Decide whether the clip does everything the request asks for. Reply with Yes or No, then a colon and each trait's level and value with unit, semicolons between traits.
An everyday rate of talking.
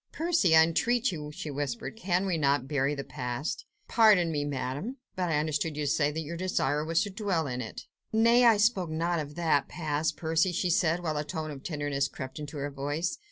No: fast, 215 wpm